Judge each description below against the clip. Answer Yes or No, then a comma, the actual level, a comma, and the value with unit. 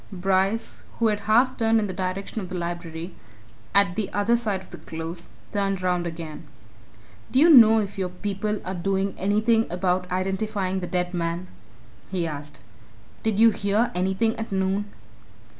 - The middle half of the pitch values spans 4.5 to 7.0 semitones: No, average, 2.9 semitones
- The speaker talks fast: No, average, 165 wpm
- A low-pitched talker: No, high, 190 Hz